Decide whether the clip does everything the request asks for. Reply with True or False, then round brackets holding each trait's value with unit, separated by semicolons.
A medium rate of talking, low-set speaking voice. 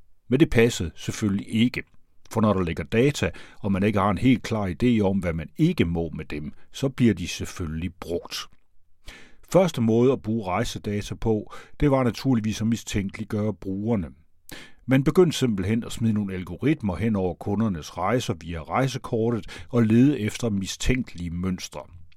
True (160 wpm; 105 Hz)